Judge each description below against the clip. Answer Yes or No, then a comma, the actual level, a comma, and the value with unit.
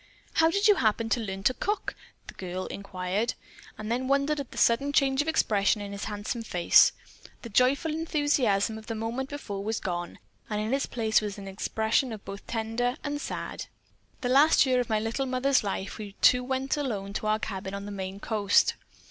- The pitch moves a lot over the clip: No, average, 4.8 semitones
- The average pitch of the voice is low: No, high, 225 Hz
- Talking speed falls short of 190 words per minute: No, average, 200 wpm